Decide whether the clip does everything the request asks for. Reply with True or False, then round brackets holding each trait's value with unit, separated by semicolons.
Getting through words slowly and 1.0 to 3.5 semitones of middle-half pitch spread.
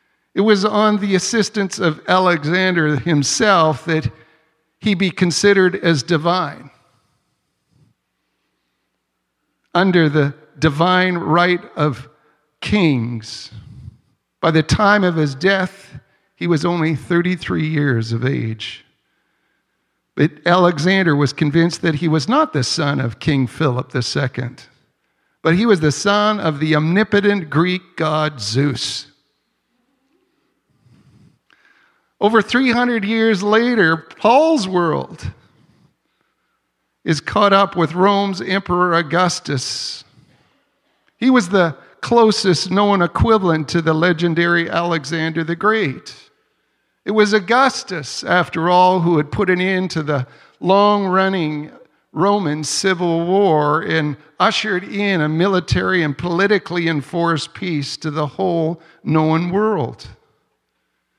False (110 wpm; 4.5 semitones)